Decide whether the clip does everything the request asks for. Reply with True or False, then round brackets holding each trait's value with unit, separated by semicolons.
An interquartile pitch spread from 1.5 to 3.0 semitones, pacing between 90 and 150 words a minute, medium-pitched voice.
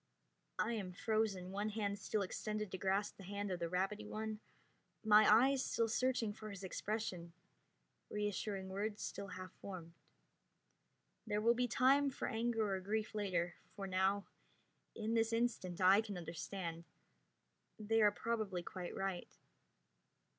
False (2.6 semitones; 140 wpm; 205 Hz)